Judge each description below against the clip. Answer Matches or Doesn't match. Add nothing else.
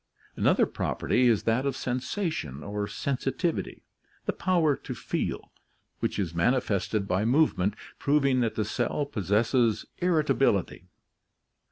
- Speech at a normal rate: Doesn't match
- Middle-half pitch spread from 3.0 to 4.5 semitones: Doesn't match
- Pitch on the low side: Matches